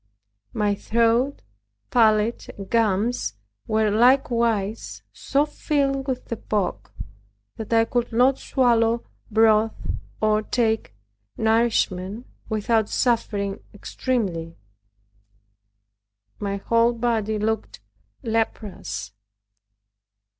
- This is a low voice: No, high, 225 Hz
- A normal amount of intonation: No, narrow, 2.2 semitones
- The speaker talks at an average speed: No, slow, 85 wpm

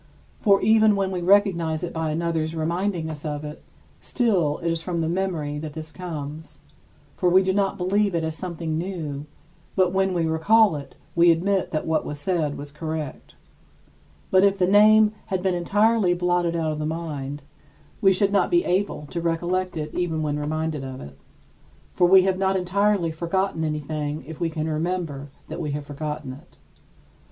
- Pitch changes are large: No, average, 3.5 semitones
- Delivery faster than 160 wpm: Yes, average, 185 wpm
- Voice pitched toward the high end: No, medium, 170 Hz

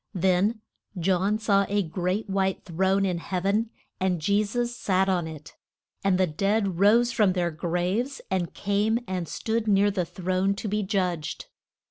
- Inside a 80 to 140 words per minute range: No, average, 165 wpm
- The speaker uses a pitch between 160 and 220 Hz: Yes, high, 190 Hz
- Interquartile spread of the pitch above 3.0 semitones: No, narrow, 2.4 semitones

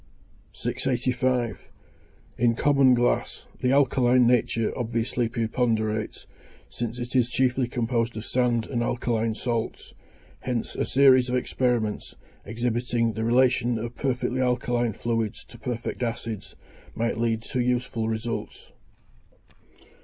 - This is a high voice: No, low, 120 Hz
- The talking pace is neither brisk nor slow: No, slow, 115 wpm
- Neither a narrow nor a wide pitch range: No, narrow, 1.6 semitones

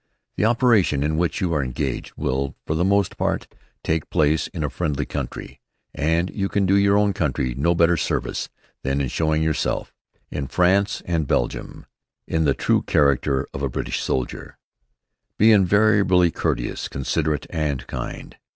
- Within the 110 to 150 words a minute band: No, average, 160 wpm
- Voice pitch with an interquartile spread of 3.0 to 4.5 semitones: No, average, 5.2 semitones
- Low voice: Yes, very low, 80 Hz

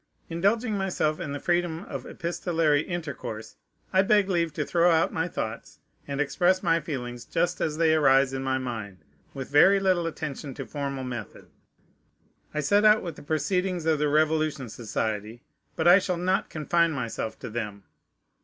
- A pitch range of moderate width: Yes, average, 4.7 semitones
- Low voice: No, medium, 155 Hz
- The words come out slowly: No, average, 170 wpm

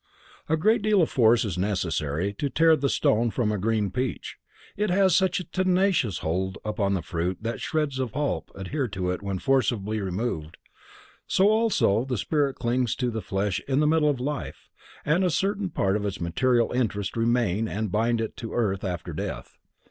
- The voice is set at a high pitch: No, low, 115 Hz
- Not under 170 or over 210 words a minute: Yes, average, 185 wpm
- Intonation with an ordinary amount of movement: No, wide, 7.1 semitones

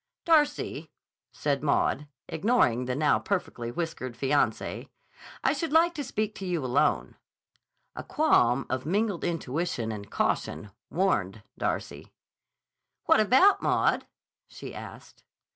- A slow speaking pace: Yes, slow, 120 wpm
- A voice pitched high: No, medium, 160 Hz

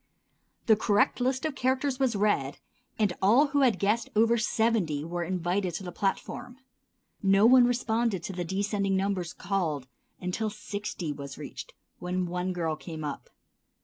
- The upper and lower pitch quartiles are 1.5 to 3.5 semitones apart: No, average, 4.5 semitones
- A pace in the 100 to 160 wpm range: Yes, average, 155 wpm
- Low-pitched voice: No, high, 200 Hz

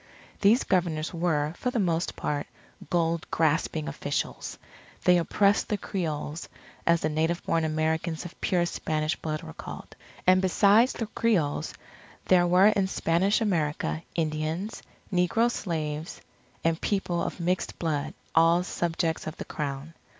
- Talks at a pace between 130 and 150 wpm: Yes, average, 140 wpm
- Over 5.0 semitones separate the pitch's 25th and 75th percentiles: No, average, 3.0 semitones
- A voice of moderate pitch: Yes, medium, 170 Hz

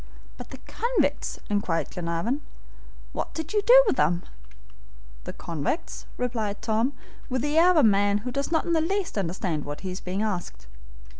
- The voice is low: No, high, 220 Hz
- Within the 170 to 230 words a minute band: Yes, average, 175 wpm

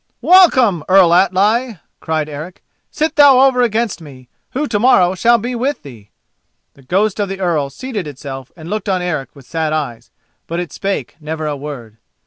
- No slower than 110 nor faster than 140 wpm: No, average, 180 wpm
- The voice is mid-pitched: Yes, medium, 180 Hz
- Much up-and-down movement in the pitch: Yes, wide, 7.6 semitones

